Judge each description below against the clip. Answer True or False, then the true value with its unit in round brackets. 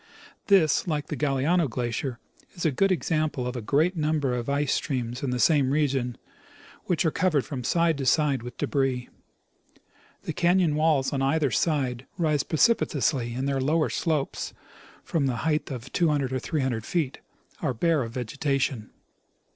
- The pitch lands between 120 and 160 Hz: True (140 Hz)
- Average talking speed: True (165 wpm)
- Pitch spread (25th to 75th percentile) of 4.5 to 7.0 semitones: False (3.6 semitones)